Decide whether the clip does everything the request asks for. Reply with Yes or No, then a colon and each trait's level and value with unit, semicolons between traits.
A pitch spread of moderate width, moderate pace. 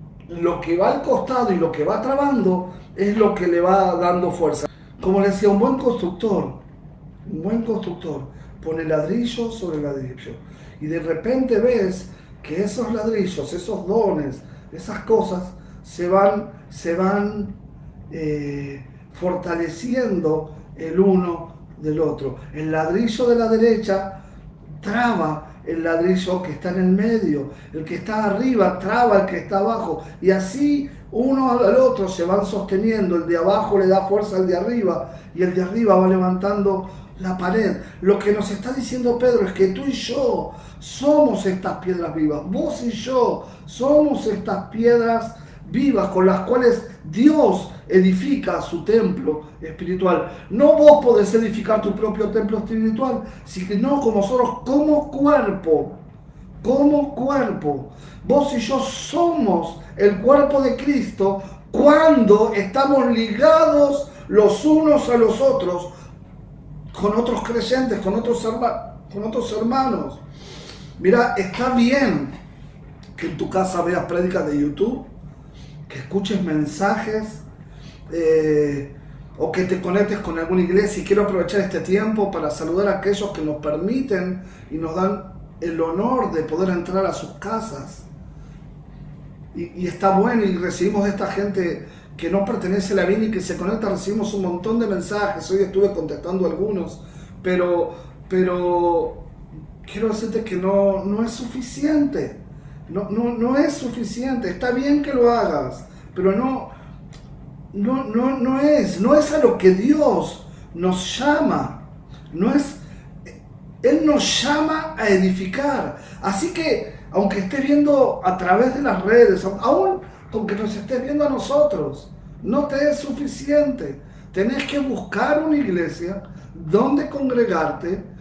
No: wide, 6.0 semitones; average, 145 wpm